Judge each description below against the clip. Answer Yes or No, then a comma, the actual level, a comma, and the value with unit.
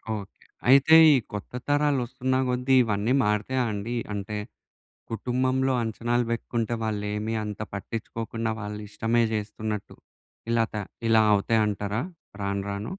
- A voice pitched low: Yes, low, 110 Hz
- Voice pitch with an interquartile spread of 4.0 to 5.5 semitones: No, average, 2.9 semitones